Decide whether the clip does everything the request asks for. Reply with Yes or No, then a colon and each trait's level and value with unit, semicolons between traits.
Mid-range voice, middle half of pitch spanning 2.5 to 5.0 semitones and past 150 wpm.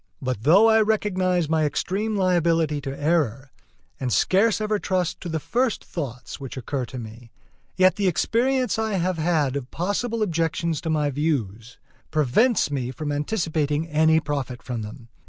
No: medium, 160 Hz; wide, 5.5 semitones; average, 160 wpm